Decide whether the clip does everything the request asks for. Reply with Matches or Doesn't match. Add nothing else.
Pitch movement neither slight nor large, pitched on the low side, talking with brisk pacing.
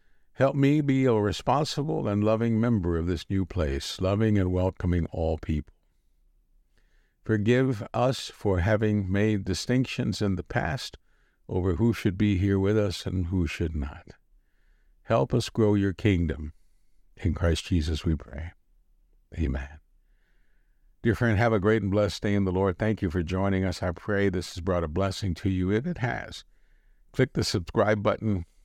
Doesn't match